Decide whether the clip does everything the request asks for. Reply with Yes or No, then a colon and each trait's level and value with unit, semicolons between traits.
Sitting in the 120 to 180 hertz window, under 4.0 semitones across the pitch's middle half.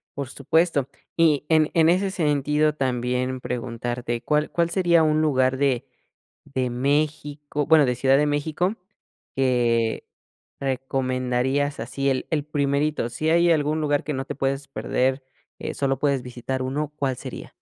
Yes: medium, 140 Hz; average, 2.9 semitones